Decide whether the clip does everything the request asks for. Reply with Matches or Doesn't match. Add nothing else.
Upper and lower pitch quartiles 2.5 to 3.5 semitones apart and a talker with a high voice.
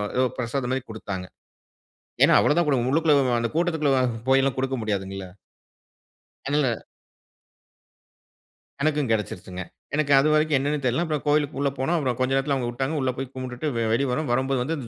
Doesn't match